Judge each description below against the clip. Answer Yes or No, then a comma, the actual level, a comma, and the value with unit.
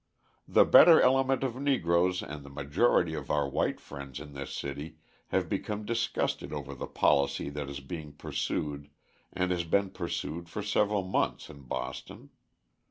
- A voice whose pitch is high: No, very low, 80 Hz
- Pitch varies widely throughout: Yes, wide, 5.9 semitones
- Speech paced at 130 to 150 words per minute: No, average, 160 wpm